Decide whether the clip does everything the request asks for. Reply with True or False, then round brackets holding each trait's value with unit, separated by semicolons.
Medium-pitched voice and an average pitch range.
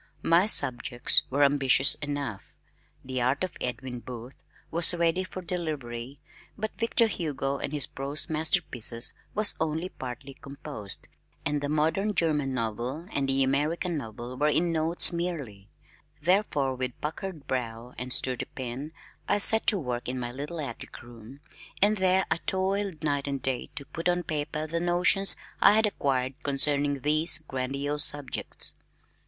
True (145 Hz; 4.6 semitones)